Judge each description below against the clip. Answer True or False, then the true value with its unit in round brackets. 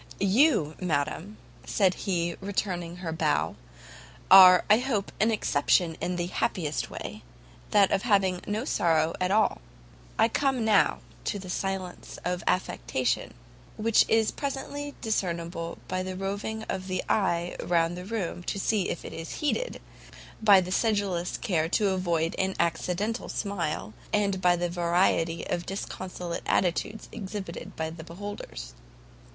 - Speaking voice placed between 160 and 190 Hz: True (185 Hz)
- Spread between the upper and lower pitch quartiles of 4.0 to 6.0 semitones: False (3.3 semitones)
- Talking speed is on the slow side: False (145 wpm)